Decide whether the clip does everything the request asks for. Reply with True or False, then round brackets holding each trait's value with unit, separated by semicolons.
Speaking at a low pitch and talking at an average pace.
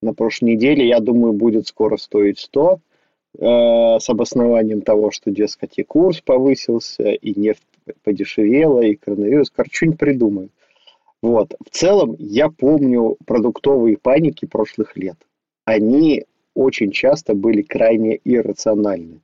True (115 Hz; 130 wpm)